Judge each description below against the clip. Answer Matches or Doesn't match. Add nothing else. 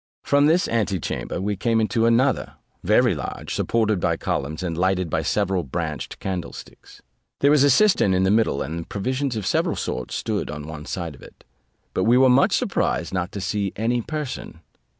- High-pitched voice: Doesn't match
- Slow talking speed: Doesn't match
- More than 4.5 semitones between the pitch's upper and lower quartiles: Matches